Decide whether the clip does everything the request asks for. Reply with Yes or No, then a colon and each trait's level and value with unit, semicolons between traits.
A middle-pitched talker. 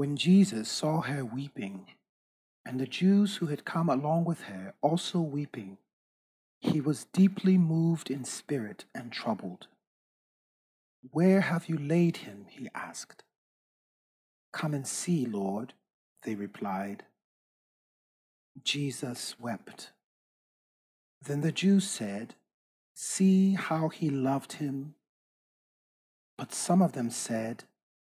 Yes: medium, 145 Hz